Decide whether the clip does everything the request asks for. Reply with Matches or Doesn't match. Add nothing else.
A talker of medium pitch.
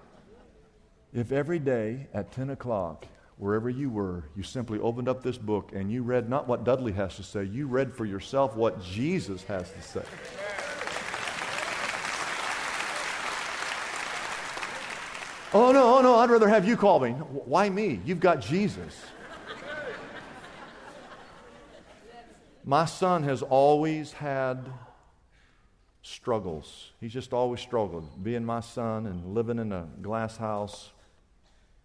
Doesn't match